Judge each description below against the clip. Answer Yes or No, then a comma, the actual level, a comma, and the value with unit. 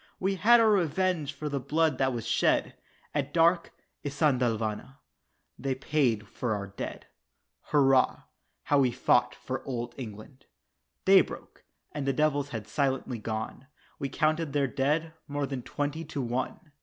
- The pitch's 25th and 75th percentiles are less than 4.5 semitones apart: Yes, average, 3.7 semitones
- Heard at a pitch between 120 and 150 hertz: Yes, medium, 140 Hz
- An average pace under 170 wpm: Yes, average, 150 wpm